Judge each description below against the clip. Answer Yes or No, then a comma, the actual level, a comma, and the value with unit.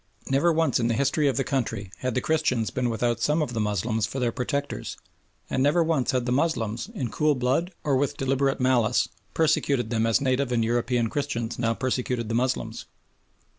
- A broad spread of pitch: No, average, 3.2 semitones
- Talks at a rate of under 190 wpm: No, average, 195 wpm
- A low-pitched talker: Yes, low, 125 Hz